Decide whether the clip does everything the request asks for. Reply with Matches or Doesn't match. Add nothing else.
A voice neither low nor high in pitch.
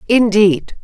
Doesn't match